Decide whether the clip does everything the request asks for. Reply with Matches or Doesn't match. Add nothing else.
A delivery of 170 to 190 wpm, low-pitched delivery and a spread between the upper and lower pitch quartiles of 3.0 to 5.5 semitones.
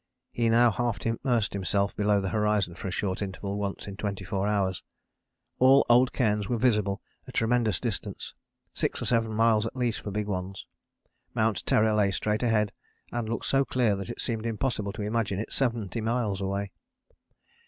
Doesn't match